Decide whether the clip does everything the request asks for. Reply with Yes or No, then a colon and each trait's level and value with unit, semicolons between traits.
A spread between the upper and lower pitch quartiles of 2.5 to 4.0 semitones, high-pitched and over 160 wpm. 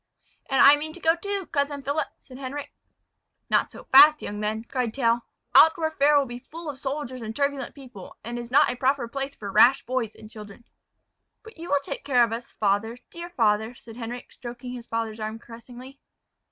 Yes: average, 3.6 semitones; very high, 255 Hz; average, 200 wpm